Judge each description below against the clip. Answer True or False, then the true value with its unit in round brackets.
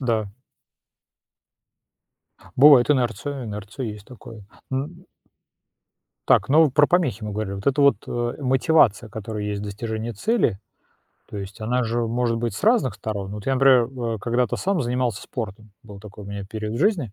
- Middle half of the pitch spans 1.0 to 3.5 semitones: False (4.0 semitones)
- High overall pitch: False (115 Hz)